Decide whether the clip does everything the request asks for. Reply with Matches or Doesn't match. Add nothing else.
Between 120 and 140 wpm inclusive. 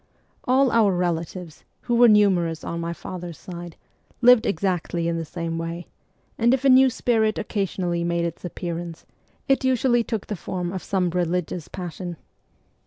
Doesn't match